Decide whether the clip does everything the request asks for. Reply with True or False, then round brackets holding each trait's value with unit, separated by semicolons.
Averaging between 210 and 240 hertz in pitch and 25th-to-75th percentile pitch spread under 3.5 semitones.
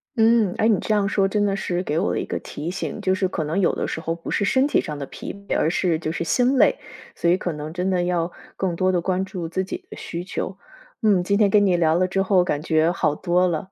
False (185 Hz; 2.7 semitones)